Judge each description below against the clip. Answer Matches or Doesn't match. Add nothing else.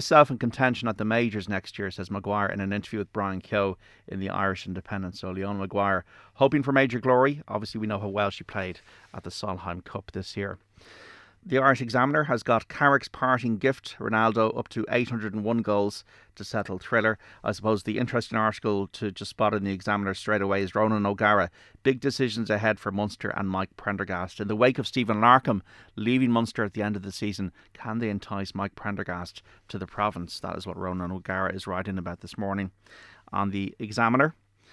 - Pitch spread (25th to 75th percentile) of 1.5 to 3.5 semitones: Matches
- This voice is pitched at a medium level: Doesn't match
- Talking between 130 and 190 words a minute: Doesn't match